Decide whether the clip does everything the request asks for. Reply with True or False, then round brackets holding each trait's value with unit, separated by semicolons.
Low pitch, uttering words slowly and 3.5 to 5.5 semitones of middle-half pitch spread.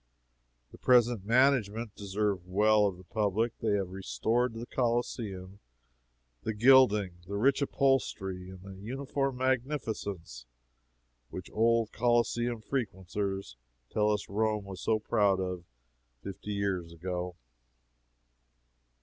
True (105 Hz; 115 wpm; 3.8 semitones)